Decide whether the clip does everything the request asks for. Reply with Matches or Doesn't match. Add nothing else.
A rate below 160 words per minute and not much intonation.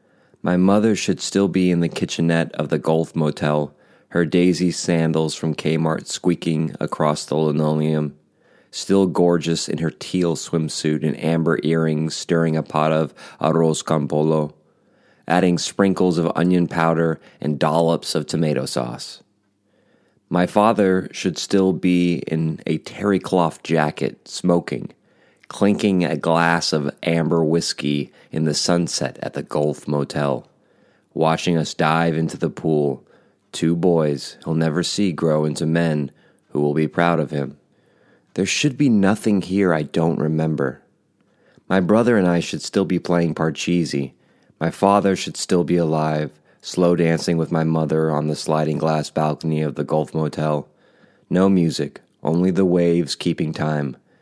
Matches